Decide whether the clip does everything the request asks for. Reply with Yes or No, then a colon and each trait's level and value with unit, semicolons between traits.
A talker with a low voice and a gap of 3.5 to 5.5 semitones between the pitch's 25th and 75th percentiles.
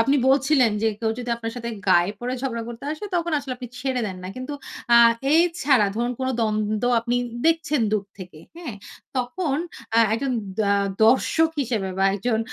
No: high, 245 Hz; average, 3.8 semitones